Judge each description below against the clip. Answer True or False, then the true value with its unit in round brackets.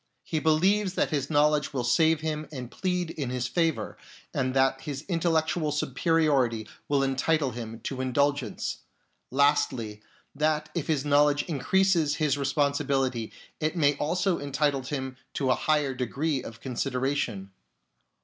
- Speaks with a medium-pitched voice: True (145 Hz)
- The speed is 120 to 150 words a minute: True (140 wpm)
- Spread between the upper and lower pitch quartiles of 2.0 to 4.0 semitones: True (3.0 semitones)